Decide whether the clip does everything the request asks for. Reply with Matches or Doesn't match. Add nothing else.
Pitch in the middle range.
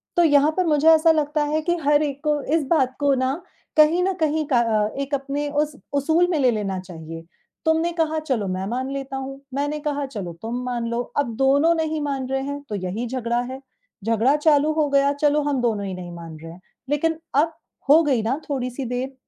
Doesn't match